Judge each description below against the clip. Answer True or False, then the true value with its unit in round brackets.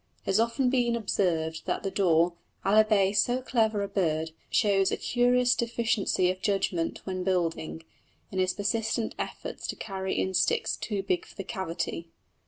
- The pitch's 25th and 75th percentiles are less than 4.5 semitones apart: True (3.6 semitones)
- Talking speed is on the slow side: False (165 wpm)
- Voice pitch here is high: True (195 Hz)